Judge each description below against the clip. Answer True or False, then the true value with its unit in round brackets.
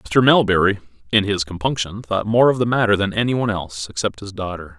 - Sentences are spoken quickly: True (215 wpm)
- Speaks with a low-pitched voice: True (100 Hz)